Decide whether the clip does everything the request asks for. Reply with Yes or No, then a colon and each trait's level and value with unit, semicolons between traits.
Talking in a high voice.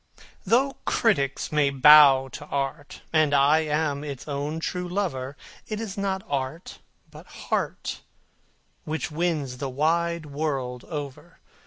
No: medium, 150 Hz